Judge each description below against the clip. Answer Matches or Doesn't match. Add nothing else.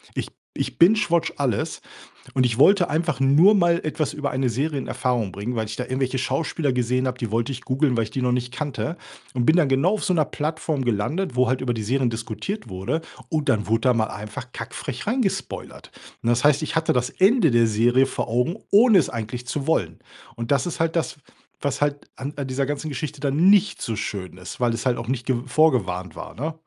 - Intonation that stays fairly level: Doesn't match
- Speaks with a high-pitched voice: Doesn't match